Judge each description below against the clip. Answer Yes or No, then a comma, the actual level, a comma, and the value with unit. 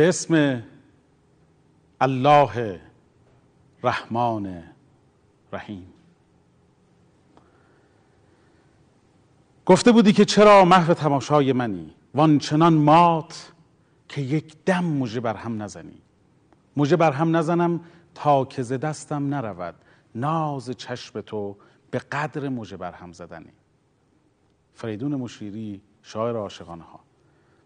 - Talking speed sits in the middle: No, slow, 95 wpm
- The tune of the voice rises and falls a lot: Yes, wide, 6.3 semitones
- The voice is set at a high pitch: No, low, 135 Hz